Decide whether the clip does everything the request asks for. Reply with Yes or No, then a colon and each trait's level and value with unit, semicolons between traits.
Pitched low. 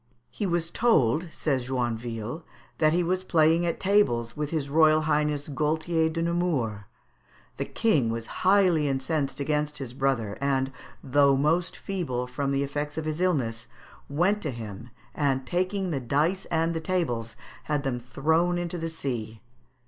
No: medium, 150 Hz